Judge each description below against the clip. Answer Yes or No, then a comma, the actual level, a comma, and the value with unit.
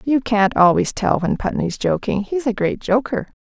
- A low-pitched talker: No, high, 220 Hz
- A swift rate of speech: No, average, 190 wpm